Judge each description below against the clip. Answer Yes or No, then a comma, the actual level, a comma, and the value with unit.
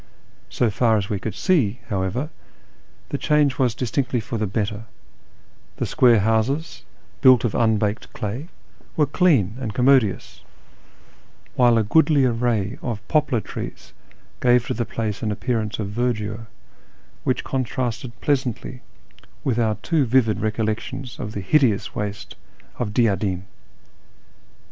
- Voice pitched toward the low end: Yes, low, 115 Hz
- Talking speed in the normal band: No, slow, 130 wpm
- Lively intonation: No, average, 3.3 semitones